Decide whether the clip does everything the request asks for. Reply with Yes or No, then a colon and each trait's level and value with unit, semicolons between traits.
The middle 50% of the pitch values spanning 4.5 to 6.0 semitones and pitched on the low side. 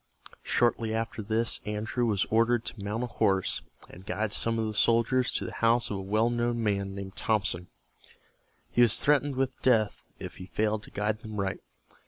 No: narrow, 2.4 semitones; low, 110 Hz